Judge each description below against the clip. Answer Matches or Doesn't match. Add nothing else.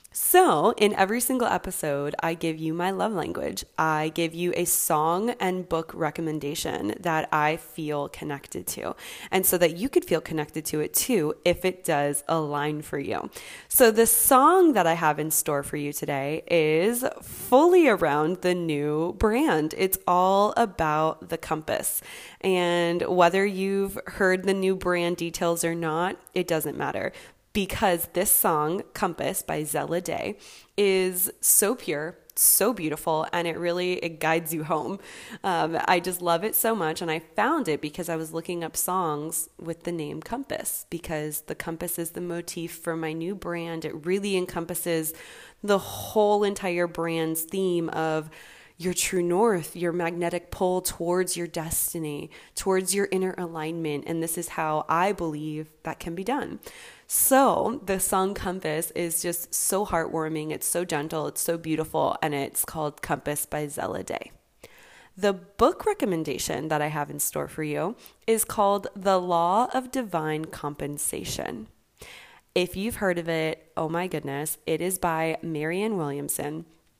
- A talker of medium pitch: Matches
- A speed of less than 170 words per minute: Matches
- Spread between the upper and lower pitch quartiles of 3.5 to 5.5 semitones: Doesn't match